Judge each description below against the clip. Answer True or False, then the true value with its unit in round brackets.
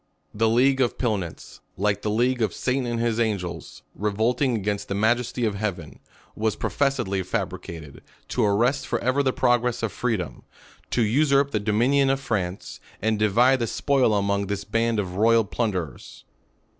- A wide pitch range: False (3.5 semitones)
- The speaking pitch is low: True (110 Hz)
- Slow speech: False (165 wpm)